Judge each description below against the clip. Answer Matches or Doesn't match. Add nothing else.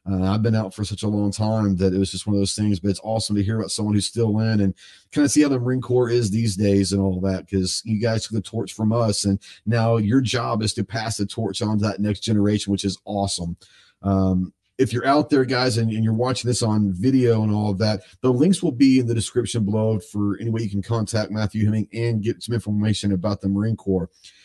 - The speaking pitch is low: Matches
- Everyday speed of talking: Doesn't match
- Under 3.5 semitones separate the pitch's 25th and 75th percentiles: Matches